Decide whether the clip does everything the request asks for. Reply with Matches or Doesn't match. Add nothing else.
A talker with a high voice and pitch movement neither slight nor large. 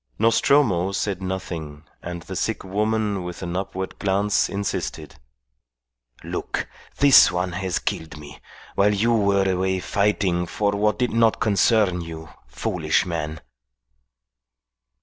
Doesn't match